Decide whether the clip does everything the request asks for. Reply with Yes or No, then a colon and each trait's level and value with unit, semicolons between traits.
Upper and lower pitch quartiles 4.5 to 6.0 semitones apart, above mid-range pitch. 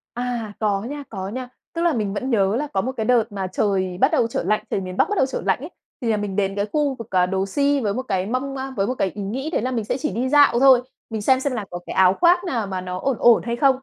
Yes: average, 5.1 semitones; high, 230 Hz